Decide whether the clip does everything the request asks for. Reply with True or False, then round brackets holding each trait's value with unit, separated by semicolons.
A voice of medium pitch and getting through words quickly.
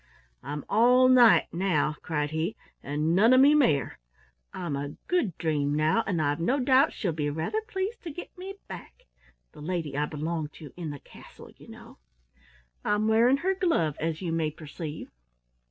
False (170 Hz; 175 wpm)